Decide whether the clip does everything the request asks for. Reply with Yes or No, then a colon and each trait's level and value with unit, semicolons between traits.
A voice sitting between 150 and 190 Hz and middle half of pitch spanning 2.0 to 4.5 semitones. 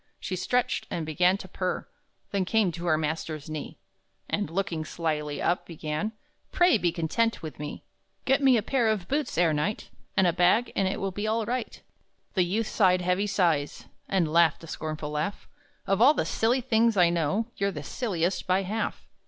No: medium, 185 Hz; average, 5.0 semitones